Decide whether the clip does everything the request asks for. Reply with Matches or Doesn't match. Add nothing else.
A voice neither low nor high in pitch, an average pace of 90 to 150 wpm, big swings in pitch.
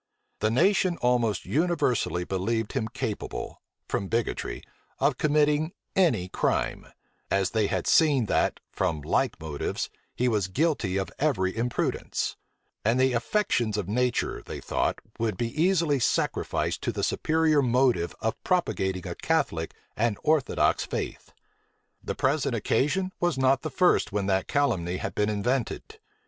Doesn't match